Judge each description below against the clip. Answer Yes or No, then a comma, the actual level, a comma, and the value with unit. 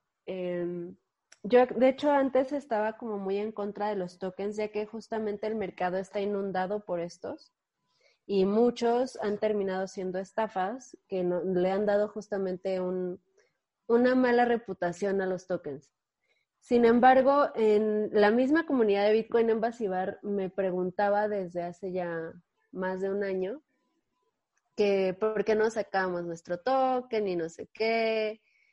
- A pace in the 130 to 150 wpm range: Yes, average, 145 wpm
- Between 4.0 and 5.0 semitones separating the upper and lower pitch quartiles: No, average, 3.5 semitones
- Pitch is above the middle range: Yes, high, 205 Hz